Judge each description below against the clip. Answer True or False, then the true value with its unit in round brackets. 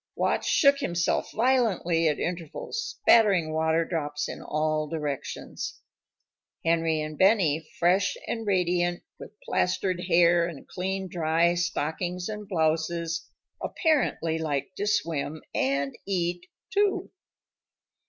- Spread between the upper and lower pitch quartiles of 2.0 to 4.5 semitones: True (3.1 semitones)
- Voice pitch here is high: False (170 Hz)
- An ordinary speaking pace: False (115 wpm)